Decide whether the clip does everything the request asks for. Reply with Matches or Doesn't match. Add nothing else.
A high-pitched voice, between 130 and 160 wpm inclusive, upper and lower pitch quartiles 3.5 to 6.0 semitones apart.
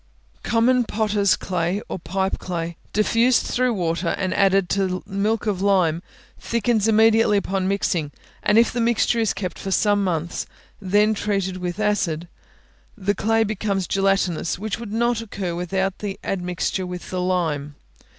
Doesn't match